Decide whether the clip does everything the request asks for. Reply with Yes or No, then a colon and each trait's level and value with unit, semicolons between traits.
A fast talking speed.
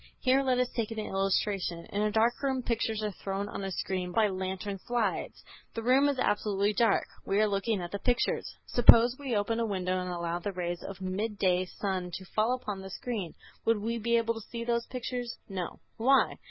Yes: fast, 210 wpm